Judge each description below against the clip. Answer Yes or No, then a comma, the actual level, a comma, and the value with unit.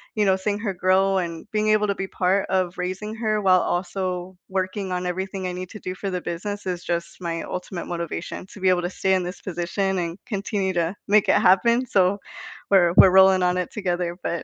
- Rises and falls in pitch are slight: Yes, narrow, 1.7 semitones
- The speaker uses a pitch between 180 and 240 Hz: Yes, medium, 185 Hz